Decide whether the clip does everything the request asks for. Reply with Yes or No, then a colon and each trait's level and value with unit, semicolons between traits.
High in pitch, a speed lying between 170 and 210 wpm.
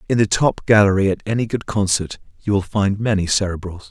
No: low, 100 Hz; average, 200 wpm